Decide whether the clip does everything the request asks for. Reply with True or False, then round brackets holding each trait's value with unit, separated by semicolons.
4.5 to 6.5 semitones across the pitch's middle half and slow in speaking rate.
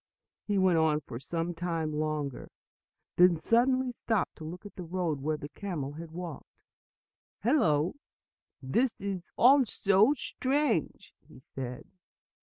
True (5.6 semitones; 130 wpm)